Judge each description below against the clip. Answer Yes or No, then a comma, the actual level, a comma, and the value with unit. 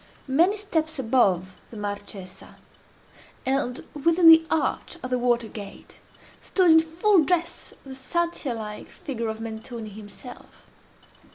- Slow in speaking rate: Yes, slow, 125 wpm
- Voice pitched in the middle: No, very high, 255 Hz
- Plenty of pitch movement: Yes, wide, 6.8 semitones